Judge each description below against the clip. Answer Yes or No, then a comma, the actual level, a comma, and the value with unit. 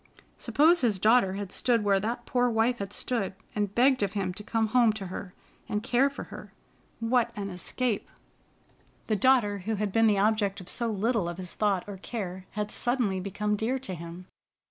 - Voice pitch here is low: No, high, 210 Hz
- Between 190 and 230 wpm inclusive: Yes, average, 195 wpm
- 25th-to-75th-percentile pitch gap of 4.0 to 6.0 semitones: No, average, 3.4 semitones